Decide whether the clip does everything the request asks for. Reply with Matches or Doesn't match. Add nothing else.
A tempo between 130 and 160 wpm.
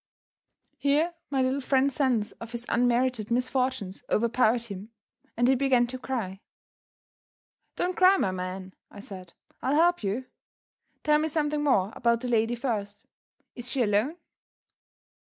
Matches